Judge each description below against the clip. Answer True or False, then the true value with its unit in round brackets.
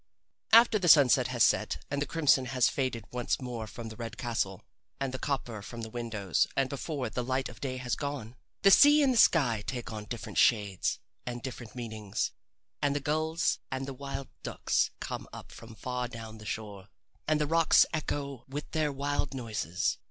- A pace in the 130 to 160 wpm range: False (190 wpm)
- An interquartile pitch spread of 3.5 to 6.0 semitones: True (4.0 semitones)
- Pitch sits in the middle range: False (125 Hz)